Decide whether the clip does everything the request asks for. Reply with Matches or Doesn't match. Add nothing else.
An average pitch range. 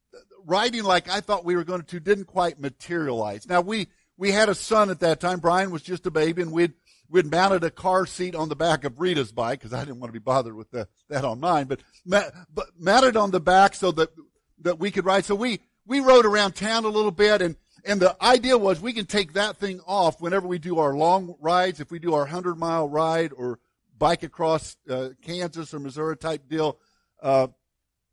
Matches